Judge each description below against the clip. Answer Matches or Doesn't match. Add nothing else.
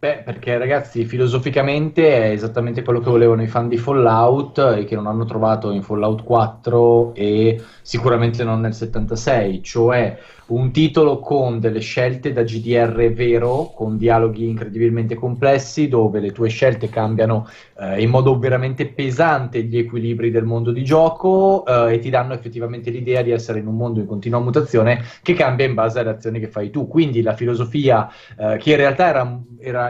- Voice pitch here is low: Matches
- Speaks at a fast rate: Matches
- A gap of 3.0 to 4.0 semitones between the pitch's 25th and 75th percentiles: Doesn't match